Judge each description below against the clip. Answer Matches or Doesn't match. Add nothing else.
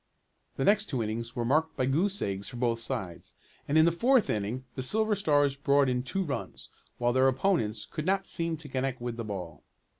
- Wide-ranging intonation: Matches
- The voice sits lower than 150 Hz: Matches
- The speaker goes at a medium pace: Doesn't match